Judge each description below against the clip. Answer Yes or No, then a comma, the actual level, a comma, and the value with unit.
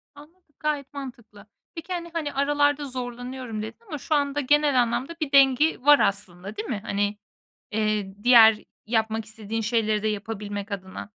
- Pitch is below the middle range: No, high, 240 Hz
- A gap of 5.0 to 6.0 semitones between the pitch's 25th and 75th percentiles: Yes, average, 5.3 semitones